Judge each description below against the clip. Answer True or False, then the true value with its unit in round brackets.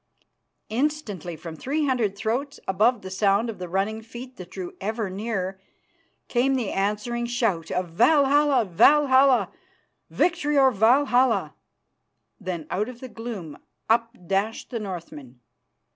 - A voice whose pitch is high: True (225 Hz)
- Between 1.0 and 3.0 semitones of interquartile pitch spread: False (5.1 semitones)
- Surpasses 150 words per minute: False (135 wpm)